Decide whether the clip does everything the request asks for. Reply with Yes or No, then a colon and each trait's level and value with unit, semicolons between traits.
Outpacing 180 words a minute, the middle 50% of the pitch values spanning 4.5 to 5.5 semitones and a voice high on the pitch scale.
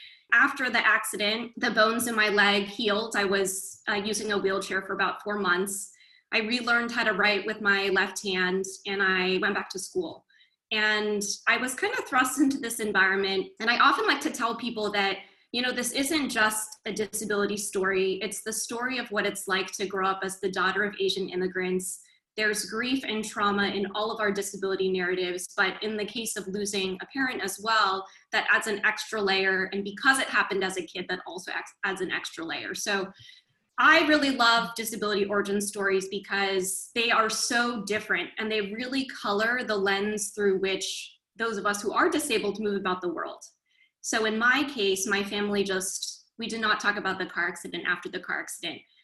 No: average, 200 wpm; average, 2.8 semitones; high, 205 Hz